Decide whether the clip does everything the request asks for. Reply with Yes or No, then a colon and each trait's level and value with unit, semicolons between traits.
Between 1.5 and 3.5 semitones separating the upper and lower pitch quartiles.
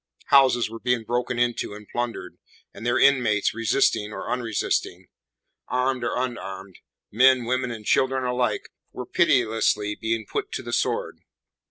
Yes: average, 2.7 semitones